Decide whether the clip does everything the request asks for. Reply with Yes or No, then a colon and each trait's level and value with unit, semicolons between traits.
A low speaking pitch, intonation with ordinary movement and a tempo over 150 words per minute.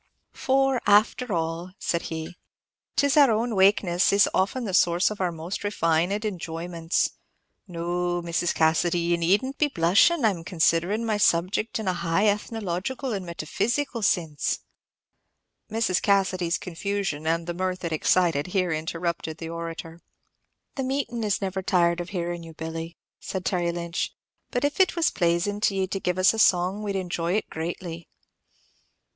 No: medium, 180 Hz; average, 3.6 semitones; average, 160 wpm